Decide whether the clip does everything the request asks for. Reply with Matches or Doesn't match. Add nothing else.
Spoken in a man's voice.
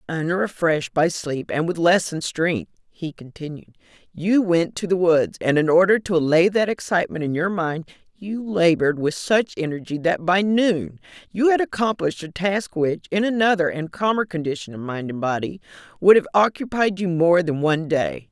Doesn't match